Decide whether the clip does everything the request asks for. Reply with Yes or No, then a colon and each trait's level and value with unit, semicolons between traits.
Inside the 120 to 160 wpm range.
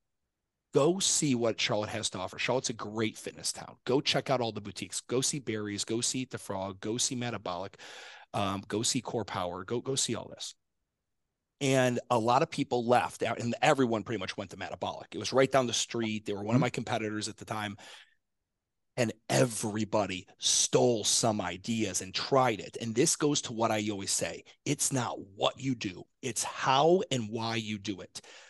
No: average, 200 wpm